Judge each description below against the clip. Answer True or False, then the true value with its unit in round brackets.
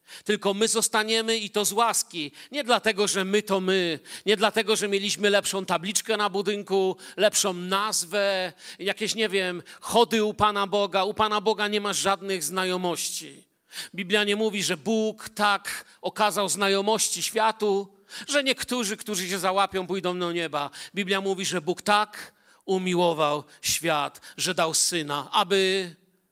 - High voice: True (200 Hz)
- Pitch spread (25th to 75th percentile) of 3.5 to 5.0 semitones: False (2.4 semitones)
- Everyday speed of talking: True (150 wpm)